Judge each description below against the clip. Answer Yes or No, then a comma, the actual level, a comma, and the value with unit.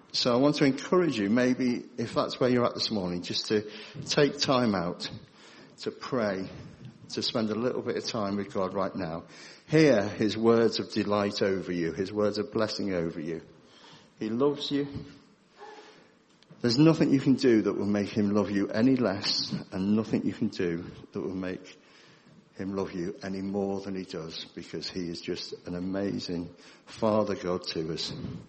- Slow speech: No, average, 185 wpm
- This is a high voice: No, low, 105 Hz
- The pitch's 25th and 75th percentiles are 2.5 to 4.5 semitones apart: No, average, 4.9 semitones